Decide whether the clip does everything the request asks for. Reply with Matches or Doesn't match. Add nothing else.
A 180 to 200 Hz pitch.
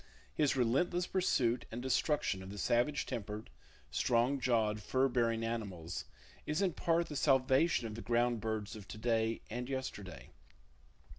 Doesn't match